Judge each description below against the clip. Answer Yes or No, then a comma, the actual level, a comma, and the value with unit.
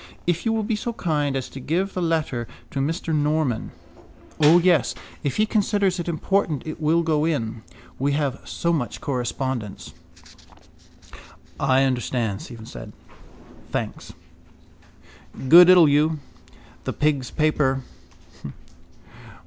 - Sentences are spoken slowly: Yes, slow, 125 wpm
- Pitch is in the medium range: Yes, medium, 150 Hz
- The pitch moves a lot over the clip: No, average, 4.2 semitones